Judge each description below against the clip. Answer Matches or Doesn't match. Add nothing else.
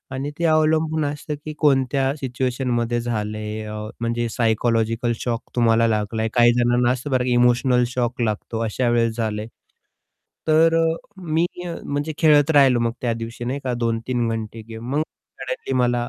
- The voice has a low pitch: Matches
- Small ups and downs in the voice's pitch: Doesn't match